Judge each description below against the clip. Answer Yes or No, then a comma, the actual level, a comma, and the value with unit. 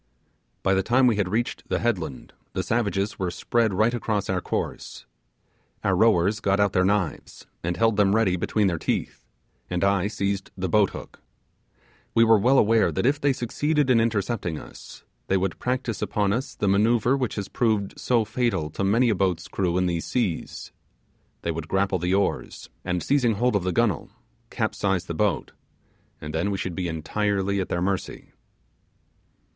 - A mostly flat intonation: No, average, 3.8 semitones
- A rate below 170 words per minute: No, average, 180 wpm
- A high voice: No, low, 100 Hz